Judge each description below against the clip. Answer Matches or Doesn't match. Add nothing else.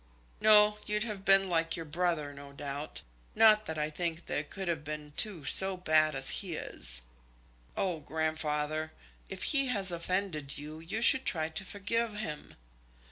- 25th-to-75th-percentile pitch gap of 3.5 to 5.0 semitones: Matches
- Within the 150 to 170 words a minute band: Matches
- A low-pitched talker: Doesn't match